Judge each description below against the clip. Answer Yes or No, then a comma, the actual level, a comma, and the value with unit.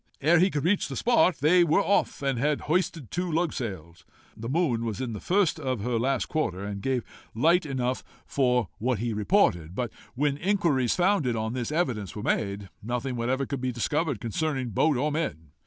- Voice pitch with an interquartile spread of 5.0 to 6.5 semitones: Yes, wide, 5.6 semitones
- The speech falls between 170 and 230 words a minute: Yes, average, 190 wpm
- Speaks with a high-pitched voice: No, low, 130 Hz